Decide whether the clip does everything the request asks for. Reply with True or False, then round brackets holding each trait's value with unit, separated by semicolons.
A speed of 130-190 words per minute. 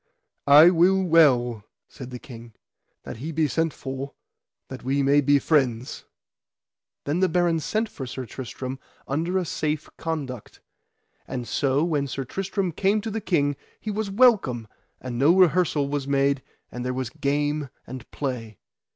True (160 wpm)